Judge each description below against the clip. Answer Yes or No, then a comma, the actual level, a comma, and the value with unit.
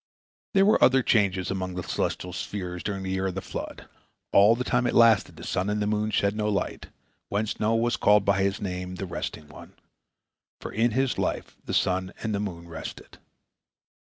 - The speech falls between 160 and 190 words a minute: No, average, 200 wpm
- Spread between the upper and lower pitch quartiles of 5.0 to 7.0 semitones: No, average, 2.7 semitones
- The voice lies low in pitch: Yes, low, 100 Hz